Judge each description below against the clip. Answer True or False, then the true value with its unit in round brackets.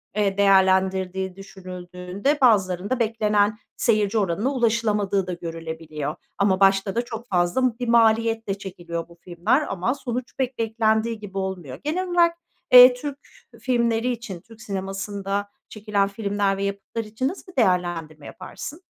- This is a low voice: False (205 Hz)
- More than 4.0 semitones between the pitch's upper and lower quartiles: False (3.6 semitones)